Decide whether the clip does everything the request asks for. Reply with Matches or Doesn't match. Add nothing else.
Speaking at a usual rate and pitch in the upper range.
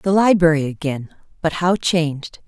Doesn't match